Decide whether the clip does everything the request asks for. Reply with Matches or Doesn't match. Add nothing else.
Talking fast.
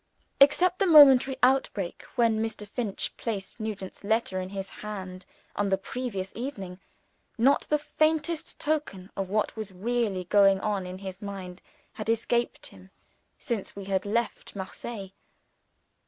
Doesn't match